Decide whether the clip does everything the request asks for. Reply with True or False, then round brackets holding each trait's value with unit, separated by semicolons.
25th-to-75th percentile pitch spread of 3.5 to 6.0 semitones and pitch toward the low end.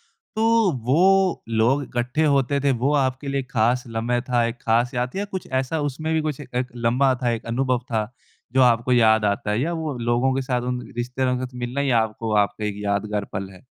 False (3.0 semitones; 125 Hz)